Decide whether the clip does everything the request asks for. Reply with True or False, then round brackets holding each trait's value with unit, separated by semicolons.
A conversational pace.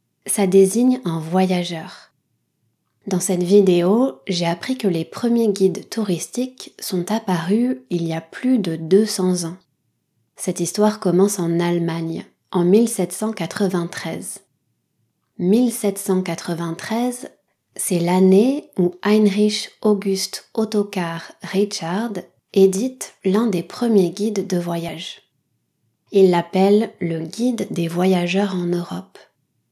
False (105 wpm)